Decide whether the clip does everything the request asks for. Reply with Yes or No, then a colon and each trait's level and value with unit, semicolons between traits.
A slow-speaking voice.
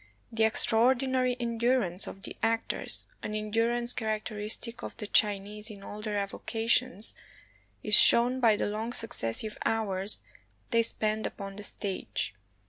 Yes: slow, 130 wpm